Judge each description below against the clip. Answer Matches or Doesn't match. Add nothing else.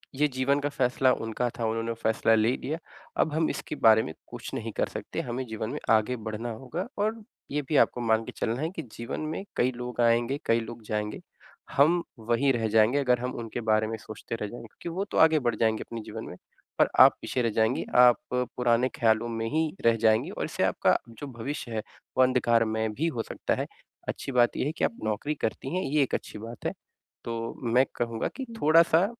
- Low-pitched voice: Matches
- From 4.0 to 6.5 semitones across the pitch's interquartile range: Doesn't match